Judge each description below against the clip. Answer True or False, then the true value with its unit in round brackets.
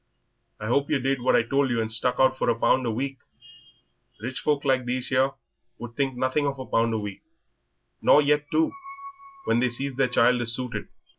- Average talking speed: False (210 wpm)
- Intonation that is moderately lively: False (2.3 semitones)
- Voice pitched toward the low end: True (130 Hz)